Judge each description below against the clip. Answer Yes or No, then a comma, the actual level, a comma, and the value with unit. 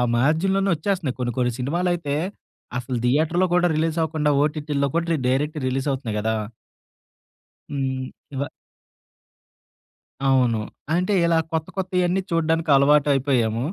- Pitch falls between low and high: Yes, medium, 150 Hz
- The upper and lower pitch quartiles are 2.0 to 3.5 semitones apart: No, average, 4.2 semitones